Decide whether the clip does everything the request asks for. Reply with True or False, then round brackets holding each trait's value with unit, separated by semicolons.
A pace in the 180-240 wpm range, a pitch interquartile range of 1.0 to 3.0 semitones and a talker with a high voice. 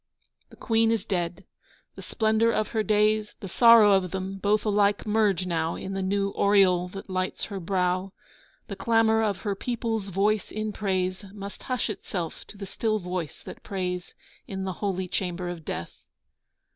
False (170 wpm; 2.6 semitones; 195 Hz)